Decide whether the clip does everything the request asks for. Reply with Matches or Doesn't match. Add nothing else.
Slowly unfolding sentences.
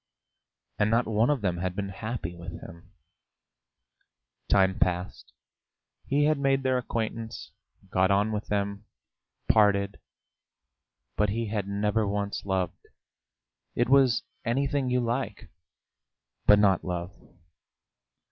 Matches